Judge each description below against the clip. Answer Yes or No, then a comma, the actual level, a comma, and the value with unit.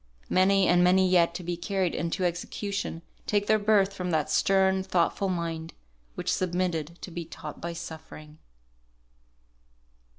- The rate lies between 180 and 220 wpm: No, average, 140 wpm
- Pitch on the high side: No, medium, 180 Hz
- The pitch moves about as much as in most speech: No, narrow, 2.2 semitones